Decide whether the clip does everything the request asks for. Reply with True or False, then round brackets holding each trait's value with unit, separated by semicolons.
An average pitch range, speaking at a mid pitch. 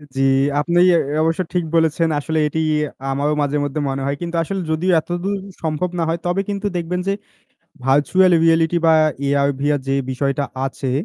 True (3.5 semitones; 160 Hz)